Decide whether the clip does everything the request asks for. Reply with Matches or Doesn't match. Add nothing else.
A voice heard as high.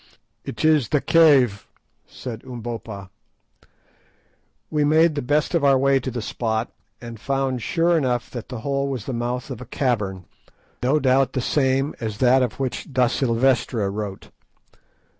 Doesn't match